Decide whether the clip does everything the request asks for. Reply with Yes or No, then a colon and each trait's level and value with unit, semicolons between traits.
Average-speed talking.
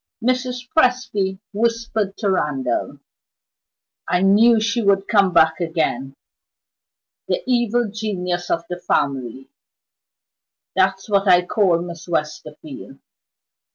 No: slow, 105 wpm